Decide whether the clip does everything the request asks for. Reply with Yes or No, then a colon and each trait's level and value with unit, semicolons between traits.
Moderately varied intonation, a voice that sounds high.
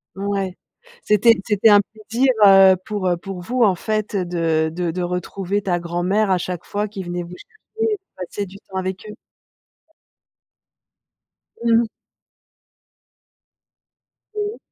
Yes: average, 3.1 semitones; high, 195 Hz